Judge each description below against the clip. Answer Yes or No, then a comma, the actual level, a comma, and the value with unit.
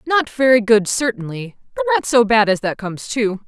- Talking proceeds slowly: No, fast, 205 wpm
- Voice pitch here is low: No, high, 230 Hz